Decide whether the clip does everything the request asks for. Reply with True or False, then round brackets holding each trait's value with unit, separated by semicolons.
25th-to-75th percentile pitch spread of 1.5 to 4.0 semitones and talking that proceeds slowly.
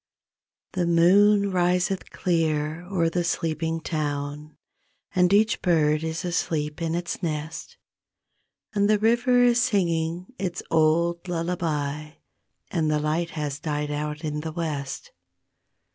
True (2.8 semitones; 130 wpm)